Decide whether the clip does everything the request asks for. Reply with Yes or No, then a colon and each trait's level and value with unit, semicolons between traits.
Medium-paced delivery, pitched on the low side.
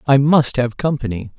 Yes: average, 175 wpm; low, 130 Hz